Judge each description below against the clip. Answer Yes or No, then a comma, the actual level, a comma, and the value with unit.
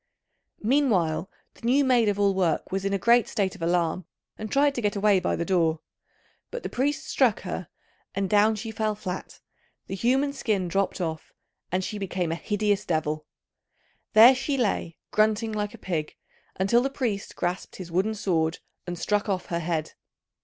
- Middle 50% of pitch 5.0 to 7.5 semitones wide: No, average, 4.0 semitones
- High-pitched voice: Yes, high, 200 Hz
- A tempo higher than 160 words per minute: Yes, average, 180 wpm